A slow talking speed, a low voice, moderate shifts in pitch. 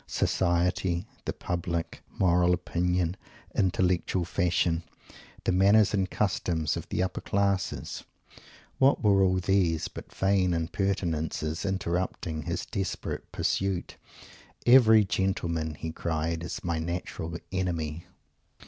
No: slow, 110 wpm; very low, 90 Hz; narrow, 2.3 semitones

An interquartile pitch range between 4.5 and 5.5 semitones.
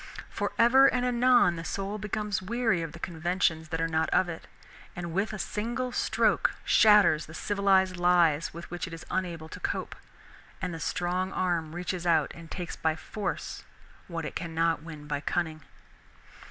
No: average, 3.5 semitones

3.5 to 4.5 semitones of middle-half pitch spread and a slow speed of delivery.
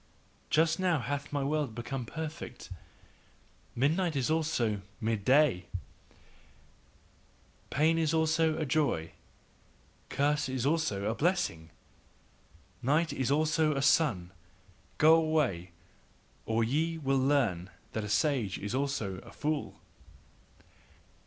No: wide, 5.5 semitones; slow, 115 wpm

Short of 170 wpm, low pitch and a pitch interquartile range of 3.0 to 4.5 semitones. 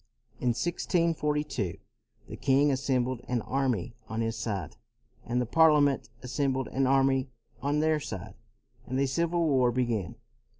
Yes: average, 140 wpm; low, 130 Hz; average, 3.5 semitones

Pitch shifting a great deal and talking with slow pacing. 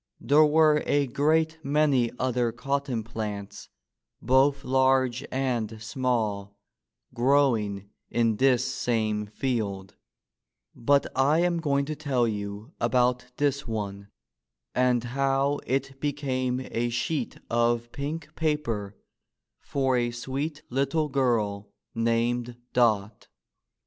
No: average, 3.5 semitones; slow, 110 wpm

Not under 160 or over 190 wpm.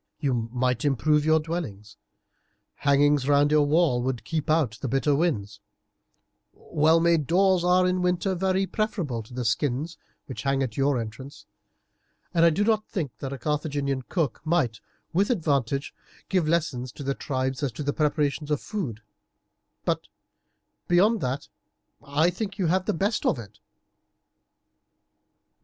No: average, 150 wpm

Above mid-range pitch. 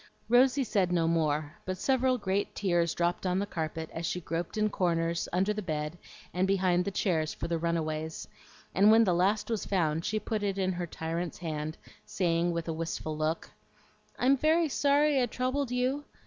No: medium, 180 Hz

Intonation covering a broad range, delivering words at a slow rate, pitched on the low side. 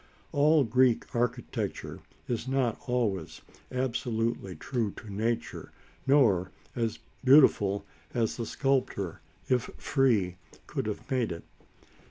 No: average, 3.5 semitones; slow, 110 wpm; low, 120 Hz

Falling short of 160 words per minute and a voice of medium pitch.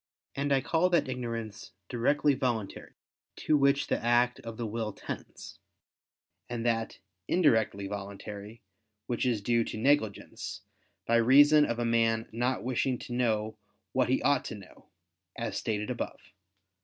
No: average, 150 wpm; low, 120 Hz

